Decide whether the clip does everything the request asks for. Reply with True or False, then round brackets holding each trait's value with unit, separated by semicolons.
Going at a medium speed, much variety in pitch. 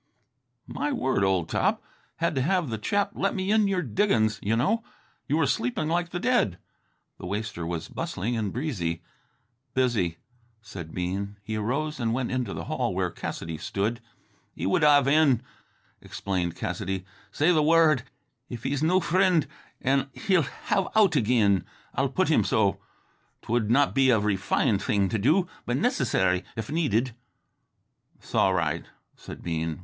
True (165 wpm; 7.8 semitones)